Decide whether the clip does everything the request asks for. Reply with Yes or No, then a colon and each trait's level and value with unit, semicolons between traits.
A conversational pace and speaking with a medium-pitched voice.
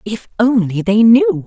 No: average, 165 wpm; high, 220 Hz